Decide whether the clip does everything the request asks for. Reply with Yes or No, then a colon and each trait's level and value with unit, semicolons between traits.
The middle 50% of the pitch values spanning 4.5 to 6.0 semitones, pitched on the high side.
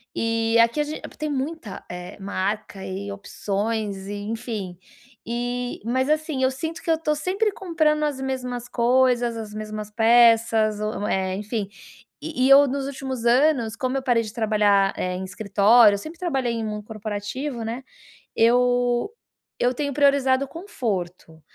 No: average, 4.1 semitones; high, 235 Hz